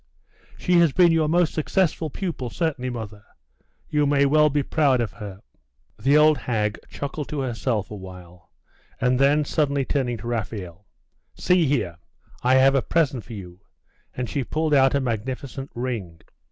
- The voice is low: Yes, low, 130 Hz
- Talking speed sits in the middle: Yes, average, 165 wpm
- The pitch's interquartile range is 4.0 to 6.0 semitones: Yes, average, 5.2 semitones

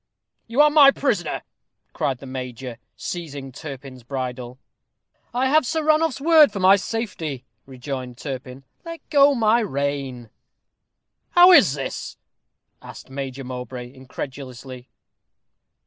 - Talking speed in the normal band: No, slow, 115 wpm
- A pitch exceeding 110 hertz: Yes, medium, 140 Hz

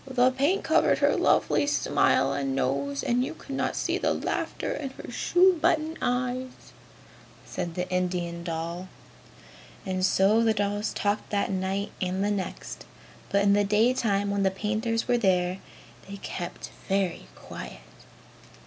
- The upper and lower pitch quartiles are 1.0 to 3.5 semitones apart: No, average, 5.1 semitones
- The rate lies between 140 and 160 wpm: Yes, average, 150 wpm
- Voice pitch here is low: No, high, 200 Hz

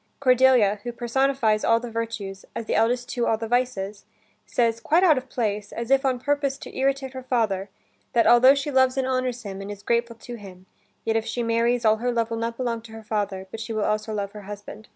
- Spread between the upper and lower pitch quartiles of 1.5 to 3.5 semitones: Yes, average, 3.0 semitones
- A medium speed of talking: No, fast, 235 wpm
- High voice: Yes, high, 230 Hz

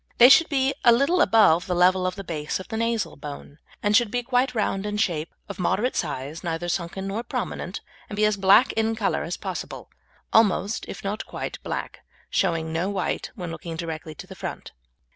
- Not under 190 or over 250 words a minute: Yes, average, 200 wpm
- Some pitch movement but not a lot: Yes, average, 5.0 semitones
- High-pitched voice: Yes, high, 195 Hz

